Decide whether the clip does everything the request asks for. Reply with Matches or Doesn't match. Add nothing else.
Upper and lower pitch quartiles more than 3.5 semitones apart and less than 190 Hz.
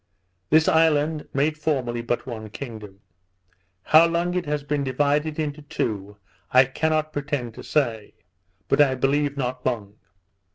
Matches